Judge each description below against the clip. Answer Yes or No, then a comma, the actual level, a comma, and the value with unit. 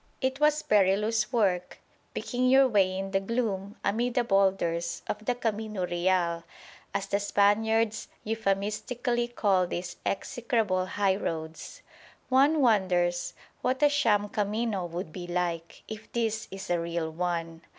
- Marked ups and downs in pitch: No, average, 4.3 semitones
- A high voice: Yes, high, 200 Hz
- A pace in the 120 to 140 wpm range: Yes, slow, 135 wpm